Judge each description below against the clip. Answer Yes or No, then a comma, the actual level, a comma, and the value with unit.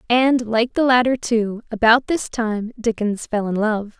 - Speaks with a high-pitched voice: Yes, high, 230 Hz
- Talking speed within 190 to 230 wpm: No, average, 180 wpm